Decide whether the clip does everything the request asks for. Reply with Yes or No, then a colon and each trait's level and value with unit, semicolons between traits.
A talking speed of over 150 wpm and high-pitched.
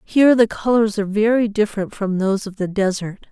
Yes: average, 200 wpm; high, 210 Hz